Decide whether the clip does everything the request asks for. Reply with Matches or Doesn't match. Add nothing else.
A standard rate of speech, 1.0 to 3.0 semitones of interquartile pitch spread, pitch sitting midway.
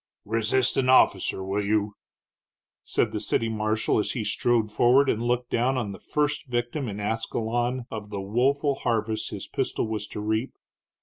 Doesn't match